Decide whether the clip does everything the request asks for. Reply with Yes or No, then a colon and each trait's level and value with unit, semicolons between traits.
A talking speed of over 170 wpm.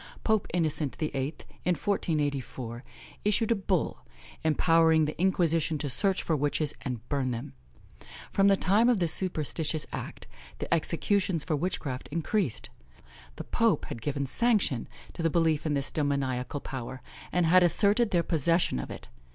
No: average, 150 wpm